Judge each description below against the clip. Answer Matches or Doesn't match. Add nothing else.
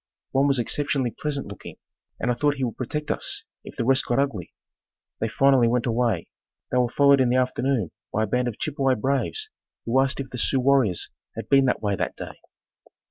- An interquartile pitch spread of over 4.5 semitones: Doesn't match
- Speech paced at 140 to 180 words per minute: Doesn't match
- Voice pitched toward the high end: Doesn't match